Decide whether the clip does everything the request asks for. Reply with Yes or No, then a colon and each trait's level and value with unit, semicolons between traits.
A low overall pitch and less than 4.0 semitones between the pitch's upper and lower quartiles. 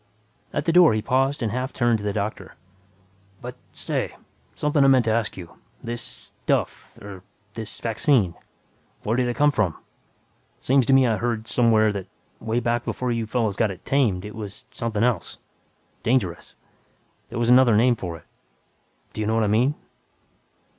Yes: low, 115 Hz; average, 3.1 semitones